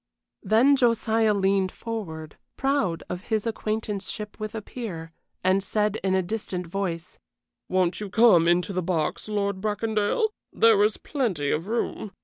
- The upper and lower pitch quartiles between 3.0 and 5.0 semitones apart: Yes, average, 3.3 semitones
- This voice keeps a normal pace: Yes, average, 145 wpm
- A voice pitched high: Yes, high, 205 Hz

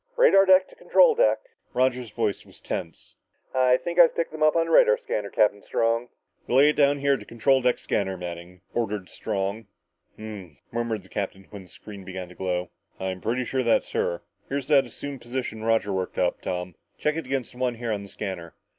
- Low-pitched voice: Yes, low, 115 Hz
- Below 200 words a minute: No, fast, 205 wpm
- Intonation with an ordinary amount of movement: No, wide, 6.3 semitones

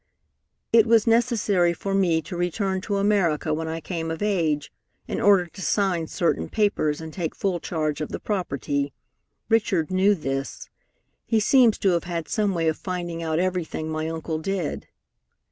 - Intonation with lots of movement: No, average, 3.8 semitones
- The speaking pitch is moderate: Yes, medium, 175 Hz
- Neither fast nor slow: Yes, average, 170 wpm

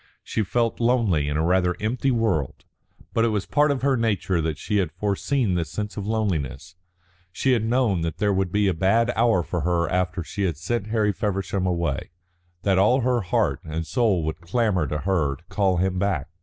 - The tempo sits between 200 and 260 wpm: Yes, fast, 205 wpm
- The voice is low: Yes, very low, 95 Hz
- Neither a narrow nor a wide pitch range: Yes, average, 4.7 semitones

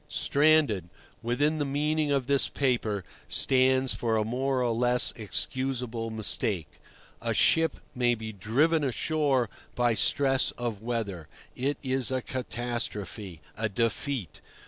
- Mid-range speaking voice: No, low, 125 Hz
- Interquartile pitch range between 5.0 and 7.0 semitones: No, average, 3.6 semitones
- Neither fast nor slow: No, slow, 125 wpm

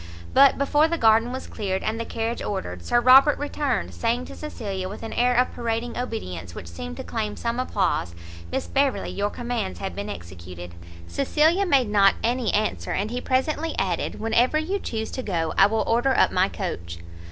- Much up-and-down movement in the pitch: No, average, 4.9 semitones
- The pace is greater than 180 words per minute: Yes, average, 190 wpm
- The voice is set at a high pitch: Yes, high, 225 Hz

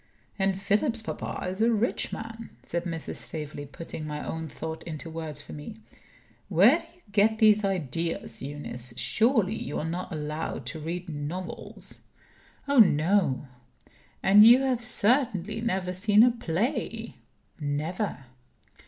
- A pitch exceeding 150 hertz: Yes, medium, 185 Hz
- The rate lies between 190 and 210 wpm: No, average, 140 wpm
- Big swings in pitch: Yes, wide, 6.0 semitones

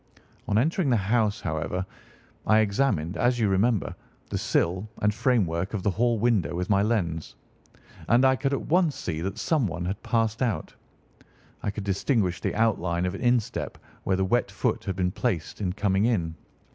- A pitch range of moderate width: Yes, average, 4.5 semitones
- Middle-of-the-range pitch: No, low, 105 Hz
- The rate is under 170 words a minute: No, average, 180 wpm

